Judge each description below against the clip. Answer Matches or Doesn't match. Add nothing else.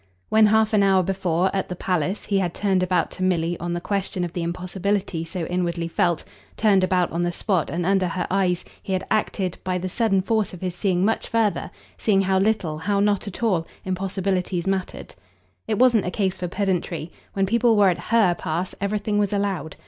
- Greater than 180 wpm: Matches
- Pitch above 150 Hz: Matches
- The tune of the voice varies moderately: Doesn't match